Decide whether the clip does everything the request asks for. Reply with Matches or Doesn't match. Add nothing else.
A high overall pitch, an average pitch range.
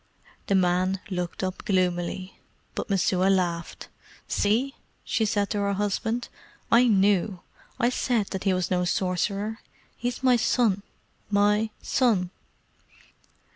Matches